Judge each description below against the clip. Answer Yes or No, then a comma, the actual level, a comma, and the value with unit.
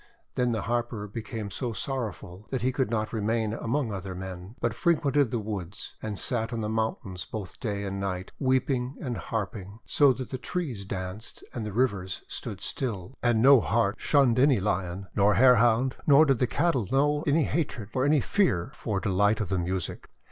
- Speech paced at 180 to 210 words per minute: Yes, average, 190 wpm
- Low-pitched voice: Yes, low, 115 Hz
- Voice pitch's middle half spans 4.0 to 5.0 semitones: Yes, average, 4.5 semitones